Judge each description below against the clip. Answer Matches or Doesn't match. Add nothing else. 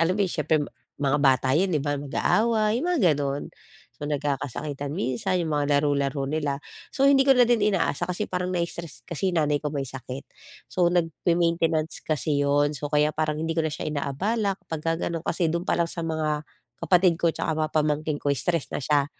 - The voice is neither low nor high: Matches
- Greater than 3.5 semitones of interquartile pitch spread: Doesn't match